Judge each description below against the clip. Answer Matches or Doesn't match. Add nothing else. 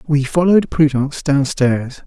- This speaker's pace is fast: Doesn't match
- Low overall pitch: Doesn't match